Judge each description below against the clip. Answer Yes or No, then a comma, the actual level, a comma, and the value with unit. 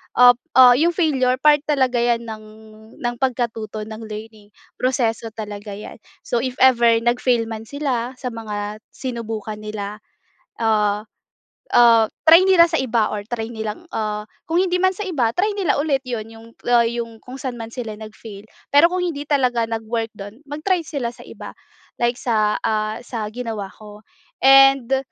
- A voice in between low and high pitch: No, high, 235 Hz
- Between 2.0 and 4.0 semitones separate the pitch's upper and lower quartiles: Yes, average, 3.6 semitones